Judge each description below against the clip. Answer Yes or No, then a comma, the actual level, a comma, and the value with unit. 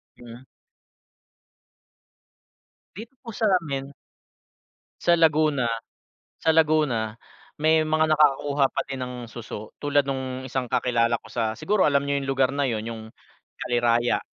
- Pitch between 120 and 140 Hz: Yes, low, 135 Hz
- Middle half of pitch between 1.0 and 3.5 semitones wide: No, average, 4.2 semitones